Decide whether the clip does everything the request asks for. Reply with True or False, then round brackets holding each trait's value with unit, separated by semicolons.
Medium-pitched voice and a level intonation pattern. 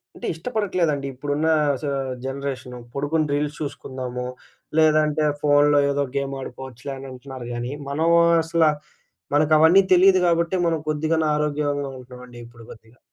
False (145 Hz; 3.1 semitones)